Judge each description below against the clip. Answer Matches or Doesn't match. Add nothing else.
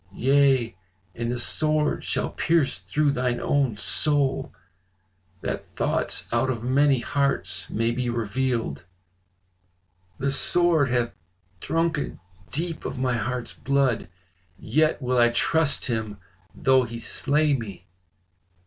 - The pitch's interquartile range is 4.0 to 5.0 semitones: Doesn't match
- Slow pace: Matches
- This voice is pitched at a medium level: Doesn't match